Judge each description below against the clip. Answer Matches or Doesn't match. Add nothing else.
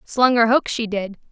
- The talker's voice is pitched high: Matches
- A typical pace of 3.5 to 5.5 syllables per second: Matches